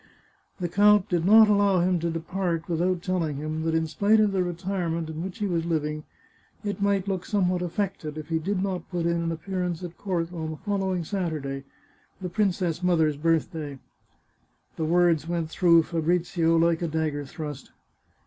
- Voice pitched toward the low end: No, medium, 170 Hz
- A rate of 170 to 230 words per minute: Yes, average, 185 wpm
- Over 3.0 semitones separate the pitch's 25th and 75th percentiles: No, narrow, 2.5 semitones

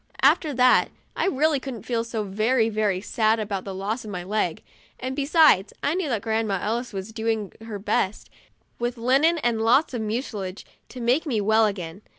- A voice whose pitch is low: No, high, 225 Hz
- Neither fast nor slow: Yes, average, 190 wpm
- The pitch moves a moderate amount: Yes, average, 3.6 semitones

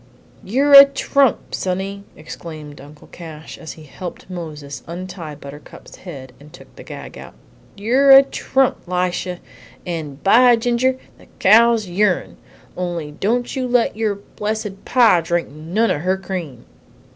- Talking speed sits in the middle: Yes, average, 145 wpm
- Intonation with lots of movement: Yes, wide, 6.5 semitones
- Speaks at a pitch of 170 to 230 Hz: Yes, medium, 185 Hz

